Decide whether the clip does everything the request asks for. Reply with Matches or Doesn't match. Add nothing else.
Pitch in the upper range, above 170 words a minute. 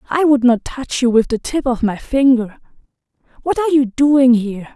Matches